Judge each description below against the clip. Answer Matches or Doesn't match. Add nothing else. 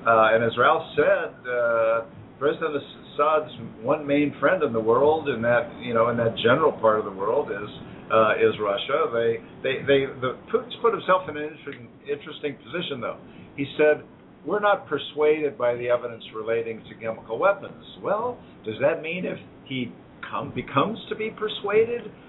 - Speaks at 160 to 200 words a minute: Matches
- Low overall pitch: Matches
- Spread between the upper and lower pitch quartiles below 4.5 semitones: Doesn't match